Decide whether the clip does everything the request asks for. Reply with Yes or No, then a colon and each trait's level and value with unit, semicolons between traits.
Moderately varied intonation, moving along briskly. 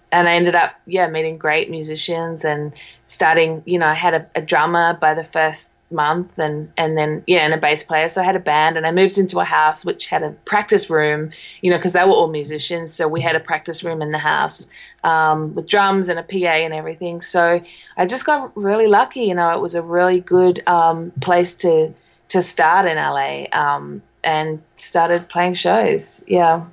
No: narrow, 2.2 semitones; fast, 215 wpm